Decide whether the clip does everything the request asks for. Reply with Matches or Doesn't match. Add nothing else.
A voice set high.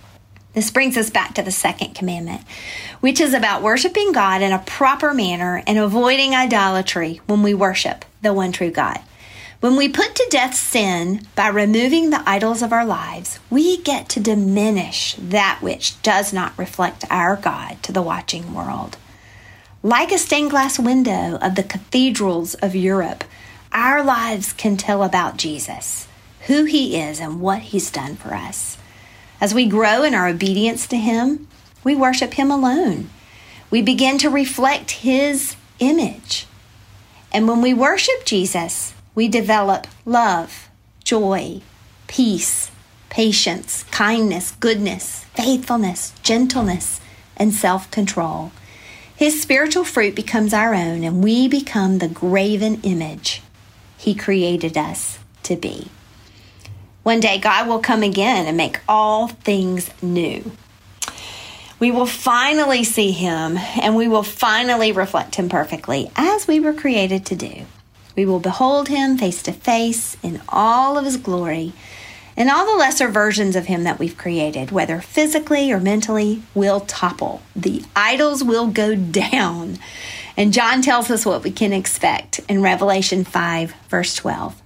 Matches